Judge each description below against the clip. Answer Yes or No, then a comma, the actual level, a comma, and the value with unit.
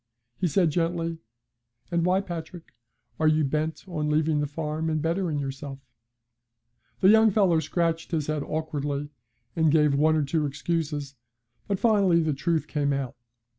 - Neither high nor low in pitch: Yes, medium, 155 Hz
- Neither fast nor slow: Yes, average, 155 wpm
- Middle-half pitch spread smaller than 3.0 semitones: Yes, narrow, 2.5 semitones